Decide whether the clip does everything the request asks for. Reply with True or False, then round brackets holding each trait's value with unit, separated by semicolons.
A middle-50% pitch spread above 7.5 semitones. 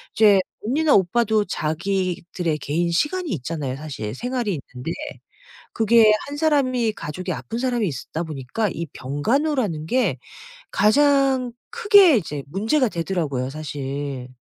True (8.7 semitones)